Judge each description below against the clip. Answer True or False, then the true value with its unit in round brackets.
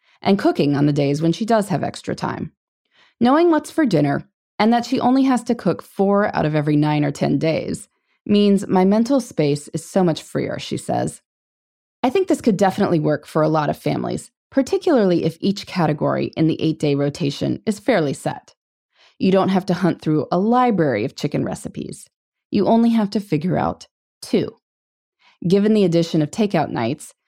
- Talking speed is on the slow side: False (190 wpm)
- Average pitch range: False (6.5 semitones)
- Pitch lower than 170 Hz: False (185 Hz)